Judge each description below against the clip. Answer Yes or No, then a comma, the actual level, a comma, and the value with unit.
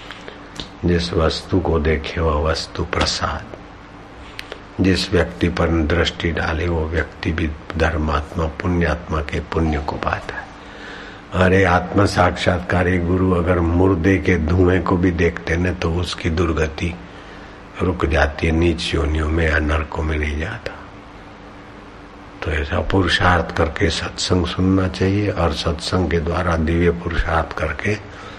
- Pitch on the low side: Yes, very low, 90 Hz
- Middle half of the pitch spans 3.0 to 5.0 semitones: No, narrow, 2.6 semitones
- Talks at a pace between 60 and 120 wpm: No, average, 130 wpm